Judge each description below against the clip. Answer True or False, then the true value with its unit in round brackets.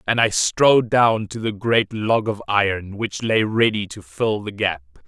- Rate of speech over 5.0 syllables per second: False (4.3 syllables/s)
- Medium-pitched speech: False (105 Hz)